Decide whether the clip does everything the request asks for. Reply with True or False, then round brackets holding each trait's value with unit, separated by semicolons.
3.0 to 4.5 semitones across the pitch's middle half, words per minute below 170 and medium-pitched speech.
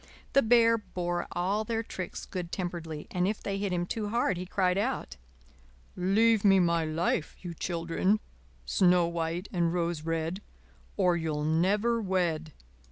True (3.3 semitones; 155 wpm; 180 Hz)